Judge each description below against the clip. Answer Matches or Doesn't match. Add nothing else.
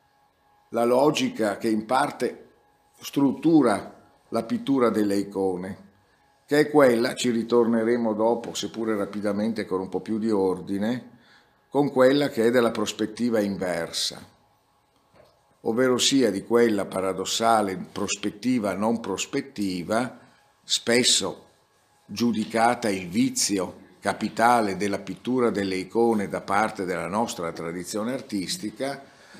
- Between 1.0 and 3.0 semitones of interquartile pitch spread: Doesn't match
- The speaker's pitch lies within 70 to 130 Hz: Matches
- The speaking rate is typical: Doesn't match